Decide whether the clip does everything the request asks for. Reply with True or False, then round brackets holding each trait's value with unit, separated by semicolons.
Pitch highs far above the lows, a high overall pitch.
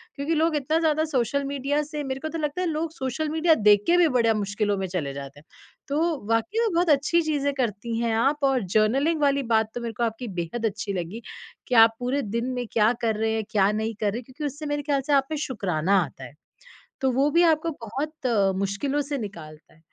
True (5.7 semitones; 255 Hz)